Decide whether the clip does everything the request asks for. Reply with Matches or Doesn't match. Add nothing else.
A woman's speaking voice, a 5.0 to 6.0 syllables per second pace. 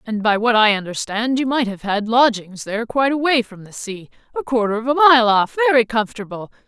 Matches